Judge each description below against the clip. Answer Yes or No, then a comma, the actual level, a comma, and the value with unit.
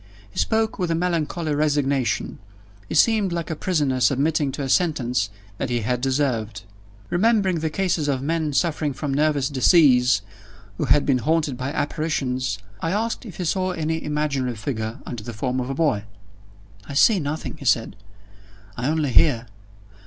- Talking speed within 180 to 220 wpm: No, average, 165 wpm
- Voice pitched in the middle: Yes, medium, 145 Hz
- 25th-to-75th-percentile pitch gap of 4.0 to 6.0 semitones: Yes, average, 4.3 semitones